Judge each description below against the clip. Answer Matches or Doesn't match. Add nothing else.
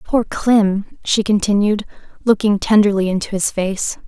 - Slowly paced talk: Matches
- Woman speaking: Matches